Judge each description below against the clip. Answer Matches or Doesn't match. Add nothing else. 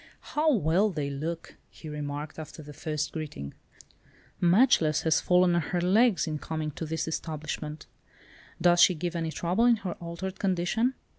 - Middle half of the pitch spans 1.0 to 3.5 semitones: Matches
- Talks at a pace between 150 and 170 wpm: Matches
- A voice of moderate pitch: Matches